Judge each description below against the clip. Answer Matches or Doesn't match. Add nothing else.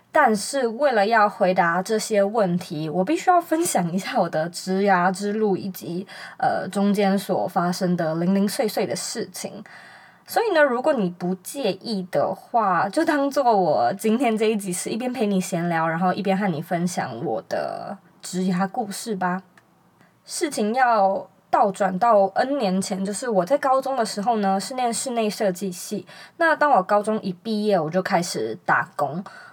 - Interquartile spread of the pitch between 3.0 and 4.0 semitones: Matches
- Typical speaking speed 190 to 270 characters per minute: Matches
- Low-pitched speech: Doesn't match